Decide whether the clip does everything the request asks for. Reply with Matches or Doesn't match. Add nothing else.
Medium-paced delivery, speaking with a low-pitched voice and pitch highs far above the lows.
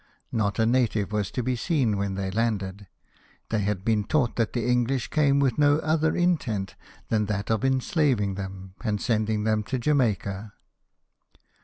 Doesn't match